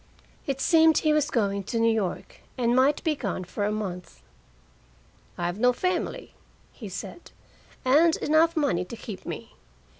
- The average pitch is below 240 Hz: No, high, 245 Hz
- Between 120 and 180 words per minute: Yes, average, 155 wpm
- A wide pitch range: Yes, wide, 7.2 semitones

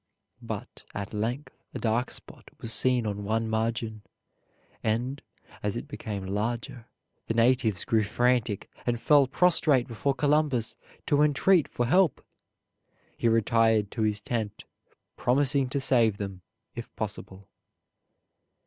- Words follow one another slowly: Yes, slow, 130 wpm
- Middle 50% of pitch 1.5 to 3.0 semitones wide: No, average, 3.4 semitones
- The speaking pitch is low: Yes, low, 115 Hz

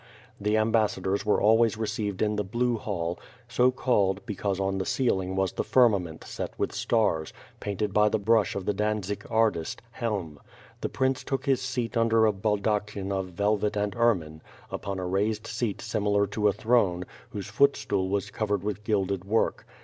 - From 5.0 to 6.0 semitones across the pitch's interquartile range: No, narrow, 2.5 semitones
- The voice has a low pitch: Yes, low, 105 Hz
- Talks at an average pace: Yes, average, 175 wpm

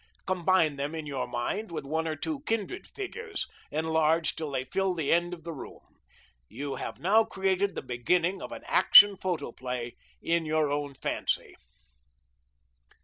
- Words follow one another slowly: No, average, 155 wpm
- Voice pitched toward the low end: No, medium, 165 Hz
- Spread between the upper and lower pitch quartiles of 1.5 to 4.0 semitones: No, average, 4.7 semitones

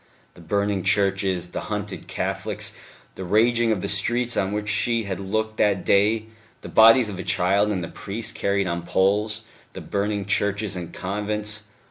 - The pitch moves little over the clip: Yes, narrow, 2.0 semitones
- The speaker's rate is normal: Yes, average, 170 wpm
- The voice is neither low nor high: No, low, 100 Hz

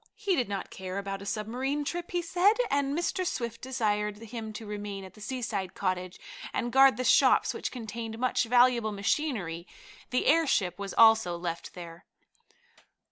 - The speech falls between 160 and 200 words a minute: Yes, average, 165 wpm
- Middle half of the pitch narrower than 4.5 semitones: No, average, 4.8 semitones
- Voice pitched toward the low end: No, high, 225 Hz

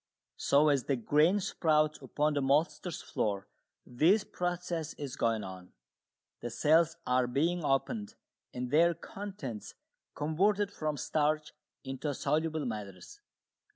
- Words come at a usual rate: No, slow, 120 wpm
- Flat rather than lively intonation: No, average, 4.7 semitones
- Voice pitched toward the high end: No, medium, 150 Hz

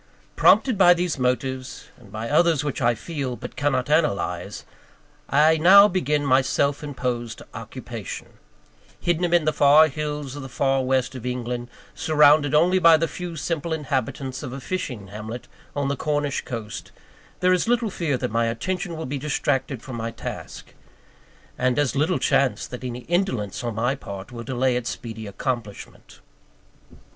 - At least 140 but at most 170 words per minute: Yes, average, 165 wpm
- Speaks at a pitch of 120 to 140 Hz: Yes, low, 135 Hz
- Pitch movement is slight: No, average, 4.2 semitones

